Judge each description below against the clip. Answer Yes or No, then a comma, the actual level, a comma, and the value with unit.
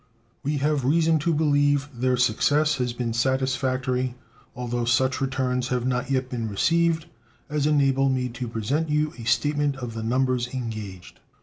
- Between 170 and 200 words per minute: No, average, 160 wpm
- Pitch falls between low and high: No, low, 130 Hz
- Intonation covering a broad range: No, average, 2.8 semitones